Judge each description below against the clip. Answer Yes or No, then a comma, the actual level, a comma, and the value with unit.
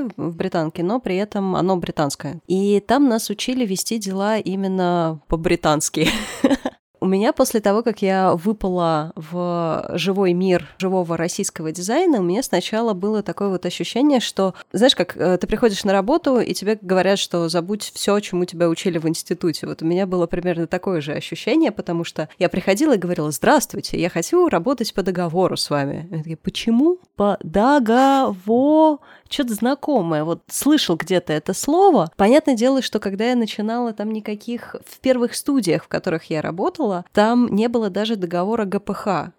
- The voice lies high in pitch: Yes, high, 195 Hz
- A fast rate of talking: Yes, fast, 165 wpm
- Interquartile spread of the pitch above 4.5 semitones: Yes, average, 5.0 semitones